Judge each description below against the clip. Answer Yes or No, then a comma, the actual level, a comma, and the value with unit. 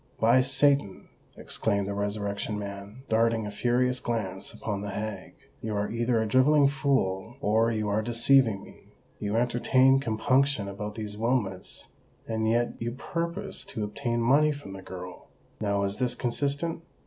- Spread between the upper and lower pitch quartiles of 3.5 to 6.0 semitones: Yes, average, 4.0 semitones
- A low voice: Yes, low, 115 Hz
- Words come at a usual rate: Yes, average, 150 wpm